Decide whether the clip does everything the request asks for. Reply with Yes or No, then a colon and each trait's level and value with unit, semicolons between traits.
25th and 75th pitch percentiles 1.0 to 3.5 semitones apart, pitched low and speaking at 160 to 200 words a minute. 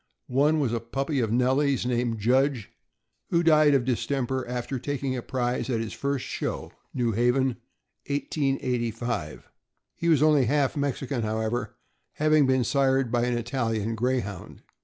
No: average, 2.9 semitones; low, 125 Hz; average, 145 wpm